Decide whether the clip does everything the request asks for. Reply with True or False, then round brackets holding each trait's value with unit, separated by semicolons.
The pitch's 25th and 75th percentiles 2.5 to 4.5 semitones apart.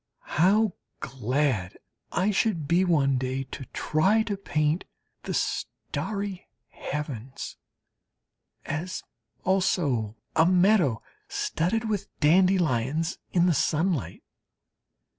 False (5.6 semitones)